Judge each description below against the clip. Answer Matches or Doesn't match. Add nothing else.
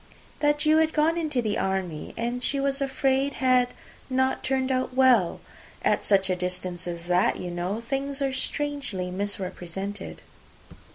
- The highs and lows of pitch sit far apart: Matches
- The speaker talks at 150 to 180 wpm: Matches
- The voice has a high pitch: Matches